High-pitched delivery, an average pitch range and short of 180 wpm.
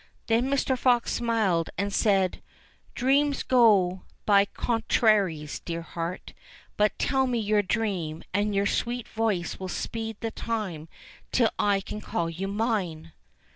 Yes: high, 210 Hz; average, 4.0 semitones; average, 145 wpm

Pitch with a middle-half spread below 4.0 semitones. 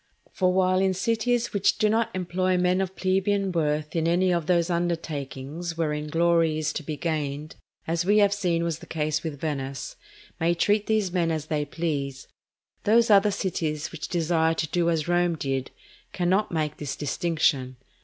Yes: average, 3.4 semitones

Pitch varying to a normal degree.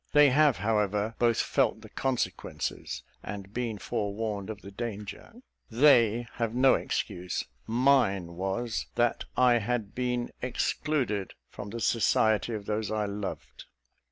Yes: average, 3.1 semitones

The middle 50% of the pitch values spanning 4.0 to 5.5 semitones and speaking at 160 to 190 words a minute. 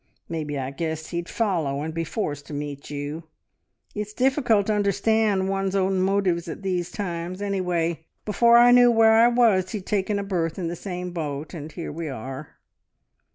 Yes: average, 4.3 semitones; average, 180 wpm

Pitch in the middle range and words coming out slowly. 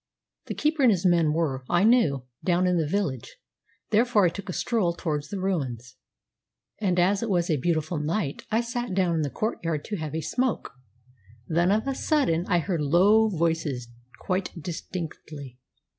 No: medium, 175 Hz; average, 175 wpm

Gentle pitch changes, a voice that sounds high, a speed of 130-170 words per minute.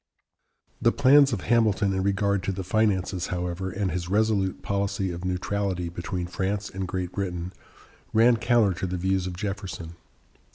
No: narrow, 2.2 semitones; very low, 95 Hz; average, 160 wpm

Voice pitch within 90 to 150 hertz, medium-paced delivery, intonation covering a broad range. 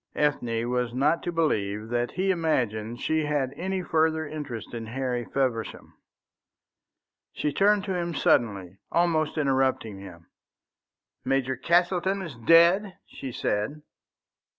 No: medium, 140 Hz; slow, 125 wpm; wide, 6.0 semitones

